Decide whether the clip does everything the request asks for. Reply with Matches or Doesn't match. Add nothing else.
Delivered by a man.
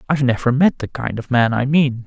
Matches